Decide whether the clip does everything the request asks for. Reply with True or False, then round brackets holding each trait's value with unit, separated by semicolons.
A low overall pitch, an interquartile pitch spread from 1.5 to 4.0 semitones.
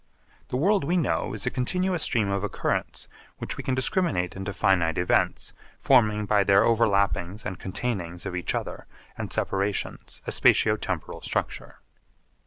False (105 Hz; 4.7 semitones)